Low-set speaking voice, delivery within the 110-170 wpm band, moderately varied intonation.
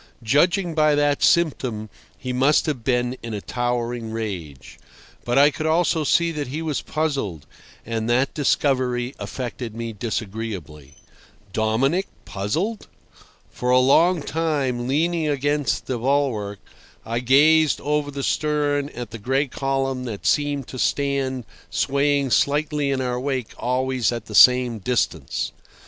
Yes: low, 130 Hz; average, 140 wpm; average, 3.8 semitones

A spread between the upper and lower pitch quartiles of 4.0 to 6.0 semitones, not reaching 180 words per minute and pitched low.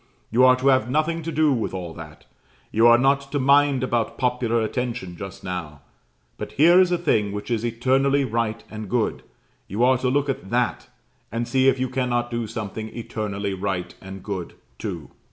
No: average, 4.3 semitones; average, 190 wpm; low, 120 Hz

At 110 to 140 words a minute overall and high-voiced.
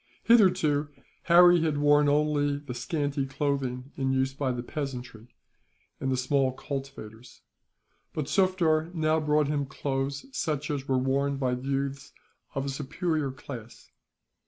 No: slow, 135 wpm; medium, 140 Hz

